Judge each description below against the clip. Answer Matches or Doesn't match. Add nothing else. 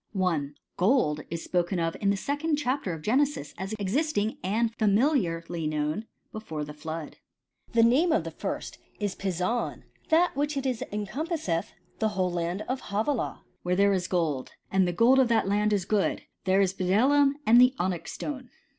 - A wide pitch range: Matches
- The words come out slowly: Doesn't match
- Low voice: Doesn't match